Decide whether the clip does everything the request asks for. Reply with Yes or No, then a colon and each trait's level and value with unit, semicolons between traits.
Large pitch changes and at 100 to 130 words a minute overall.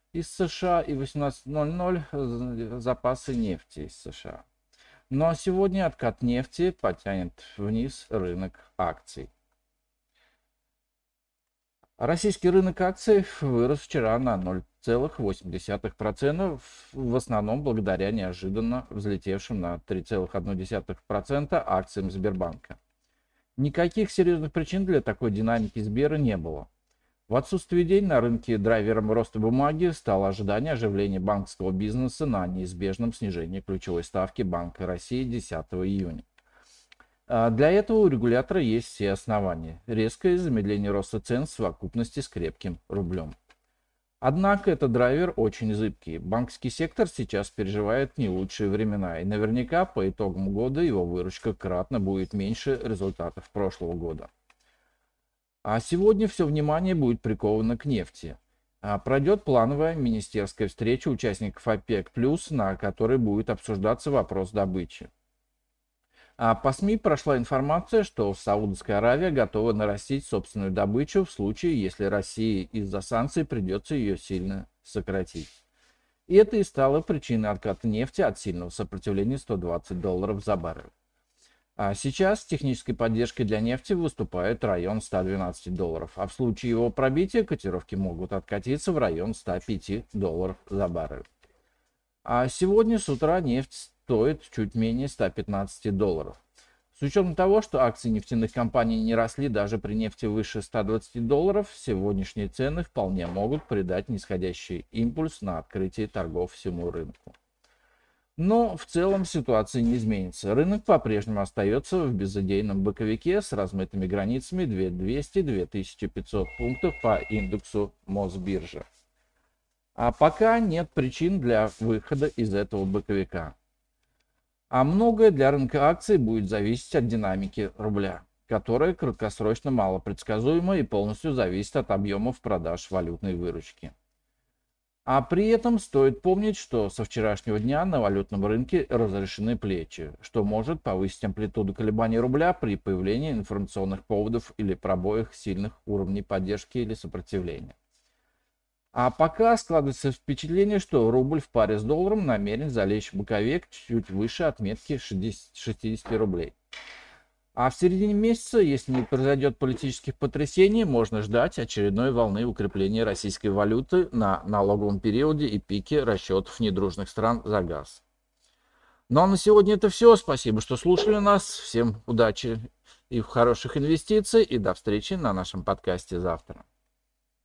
Yes: wide, 6.1 semitones; average, 125 wpm